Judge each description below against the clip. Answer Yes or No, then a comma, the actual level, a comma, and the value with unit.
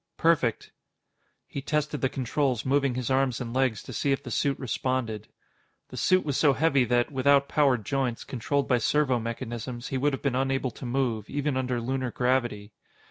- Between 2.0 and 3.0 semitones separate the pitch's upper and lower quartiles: Yes, narrow, 2.5 semitones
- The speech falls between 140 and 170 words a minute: No, average, 180 wpm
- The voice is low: Yes, low, 130 Hz